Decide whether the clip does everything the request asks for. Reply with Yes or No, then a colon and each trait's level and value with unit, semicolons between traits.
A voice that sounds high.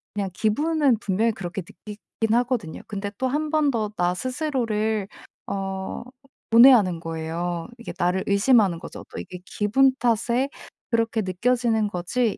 Yes: high, 215 Hz